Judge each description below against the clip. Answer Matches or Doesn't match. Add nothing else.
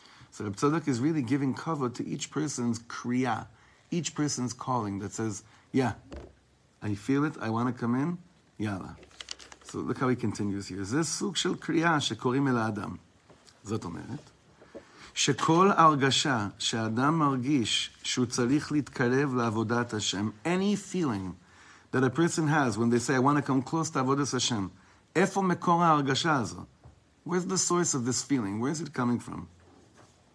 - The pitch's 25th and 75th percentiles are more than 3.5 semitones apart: Matches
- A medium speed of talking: Matches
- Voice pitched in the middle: Doesn't match